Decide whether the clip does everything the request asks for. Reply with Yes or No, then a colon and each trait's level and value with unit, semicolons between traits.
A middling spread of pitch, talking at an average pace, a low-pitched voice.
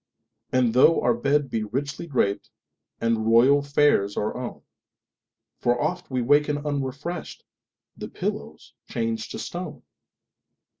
No: average, 3.9 semitones; slow, 105 wpm; low, 130 Hz